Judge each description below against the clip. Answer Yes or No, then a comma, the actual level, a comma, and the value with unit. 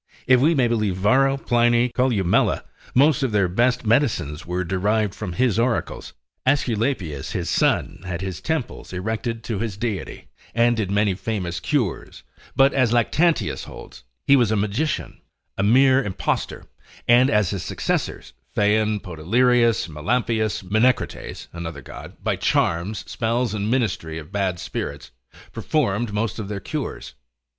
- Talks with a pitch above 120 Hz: No, low, 110 Hz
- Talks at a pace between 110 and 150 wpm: Yes, average, 145 wpm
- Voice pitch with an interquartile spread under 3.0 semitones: No, average, 4.5 semitones